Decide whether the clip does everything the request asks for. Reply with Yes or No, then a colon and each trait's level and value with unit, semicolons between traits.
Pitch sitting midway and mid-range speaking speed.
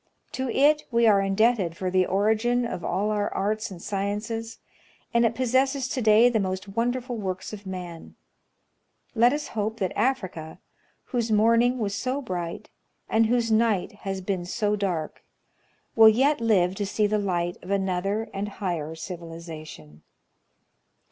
No: high, 210 Hz; average, 155 wpm